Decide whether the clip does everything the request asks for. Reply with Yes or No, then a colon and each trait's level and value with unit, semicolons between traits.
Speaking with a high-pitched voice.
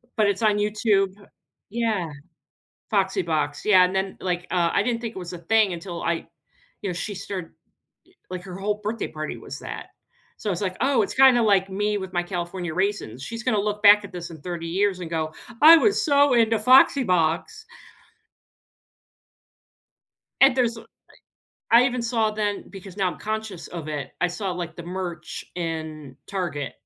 Yes: high, 195 Hz